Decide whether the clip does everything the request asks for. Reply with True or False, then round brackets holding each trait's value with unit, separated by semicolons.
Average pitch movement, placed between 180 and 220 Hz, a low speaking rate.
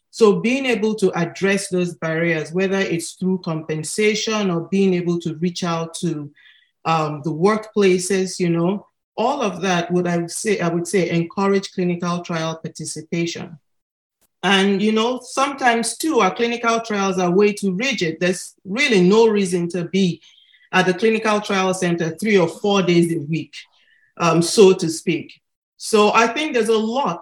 False (3.7 semitones; 185 Hz; 170 wpm)